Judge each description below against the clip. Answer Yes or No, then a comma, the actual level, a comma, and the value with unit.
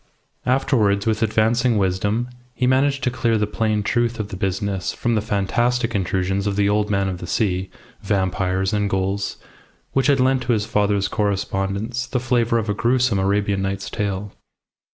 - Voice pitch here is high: No, low, 105 Hz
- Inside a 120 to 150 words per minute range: No, average, 175 wpm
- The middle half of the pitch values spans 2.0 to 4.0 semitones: Yes, average, 3.4 semitones